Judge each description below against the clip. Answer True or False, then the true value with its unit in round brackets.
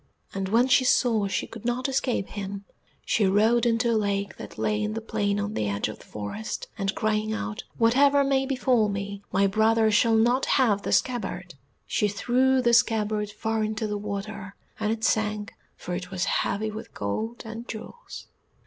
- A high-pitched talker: True (215 Hz)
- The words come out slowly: False (185 wpm)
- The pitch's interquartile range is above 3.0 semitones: False (2.6 semitones)